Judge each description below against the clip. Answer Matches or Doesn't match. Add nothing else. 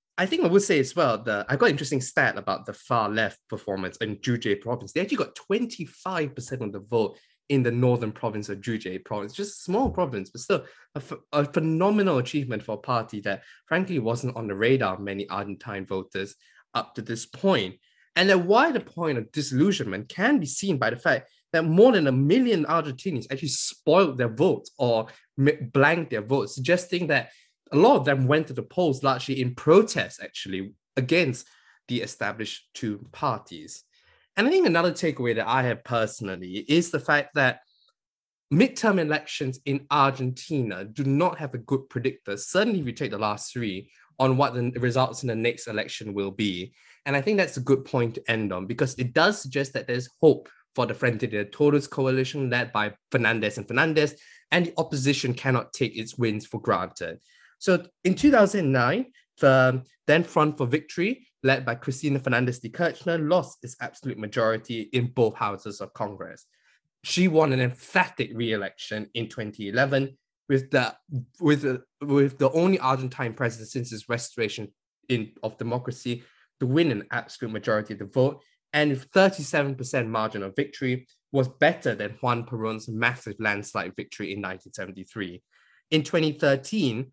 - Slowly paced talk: Doesn't match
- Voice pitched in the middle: Doesn't match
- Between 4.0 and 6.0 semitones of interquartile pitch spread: Matches